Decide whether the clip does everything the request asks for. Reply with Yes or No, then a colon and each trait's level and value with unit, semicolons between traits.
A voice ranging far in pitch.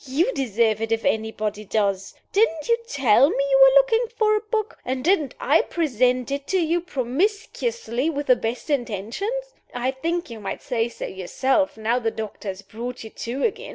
Yes: wide, 8.7 semitones